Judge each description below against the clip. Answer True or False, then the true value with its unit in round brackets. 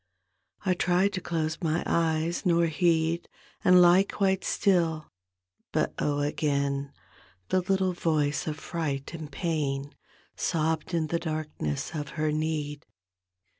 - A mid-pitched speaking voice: True (160 Hz)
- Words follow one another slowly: True (130 wpm)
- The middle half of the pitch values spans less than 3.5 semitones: True (2.6 semitones)